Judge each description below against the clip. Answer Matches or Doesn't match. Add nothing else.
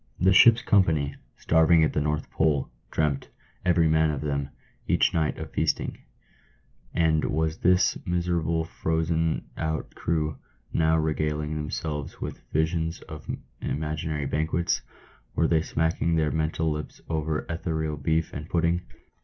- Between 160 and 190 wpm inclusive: Doesn't match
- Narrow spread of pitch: Matches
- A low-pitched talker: Matches